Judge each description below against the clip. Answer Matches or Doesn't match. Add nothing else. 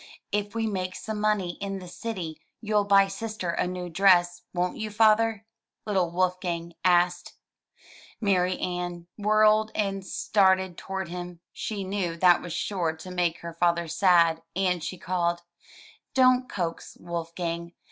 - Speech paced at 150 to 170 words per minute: Doesn't match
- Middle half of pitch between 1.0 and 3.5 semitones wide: Matches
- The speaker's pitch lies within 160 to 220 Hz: Matches